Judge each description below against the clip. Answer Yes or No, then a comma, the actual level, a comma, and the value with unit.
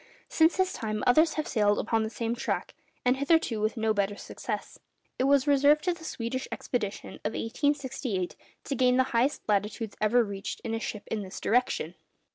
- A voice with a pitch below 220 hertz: No, high, 235 Hz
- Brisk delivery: No, average, 185 wpm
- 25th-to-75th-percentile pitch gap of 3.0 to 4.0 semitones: No, average, 4.6 semitones